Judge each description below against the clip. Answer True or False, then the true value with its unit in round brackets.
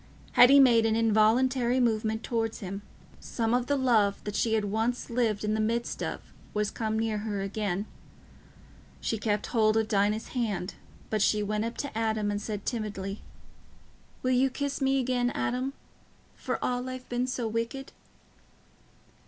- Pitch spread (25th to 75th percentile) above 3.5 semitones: False (2.7 semitones)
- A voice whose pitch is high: True (225 Hz)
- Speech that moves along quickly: False (160 wpm)